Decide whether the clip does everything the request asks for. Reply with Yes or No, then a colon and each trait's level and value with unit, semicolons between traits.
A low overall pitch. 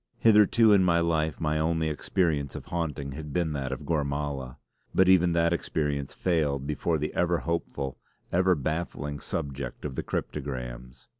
Yes: very low, 75 Hz